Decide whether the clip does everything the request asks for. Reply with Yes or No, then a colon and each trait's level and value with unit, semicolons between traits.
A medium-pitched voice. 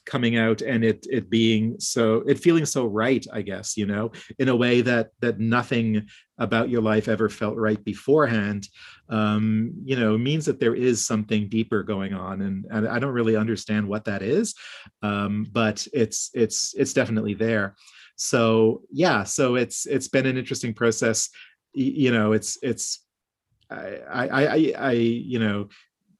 No: low, 115 Hz